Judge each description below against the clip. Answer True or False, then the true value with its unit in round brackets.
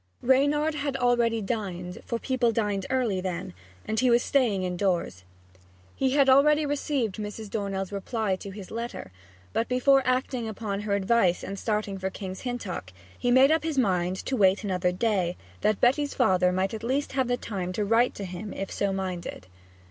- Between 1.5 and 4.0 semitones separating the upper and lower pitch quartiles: False (4.9 semitones)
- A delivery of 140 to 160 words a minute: False (180 wpm)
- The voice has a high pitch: True (215 Hz)